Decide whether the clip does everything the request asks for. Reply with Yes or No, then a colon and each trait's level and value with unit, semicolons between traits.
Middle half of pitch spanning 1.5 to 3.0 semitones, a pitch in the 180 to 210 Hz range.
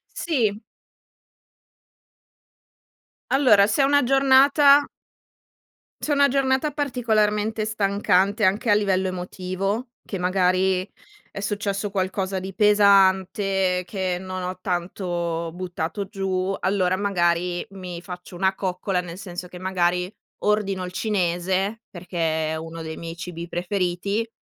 Yes: narrow, 2.6 semitones; high, 190 Hz